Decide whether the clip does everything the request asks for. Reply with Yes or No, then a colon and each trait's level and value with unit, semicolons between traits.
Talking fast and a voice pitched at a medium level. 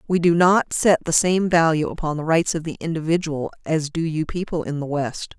Yes: fast, 225 wpm; medium, 160 Hz